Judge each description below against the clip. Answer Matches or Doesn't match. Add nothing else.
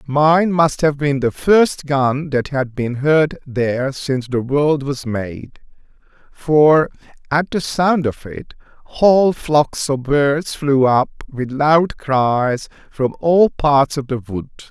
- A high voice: Doesn't match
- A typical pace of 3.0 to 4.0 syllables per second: Matches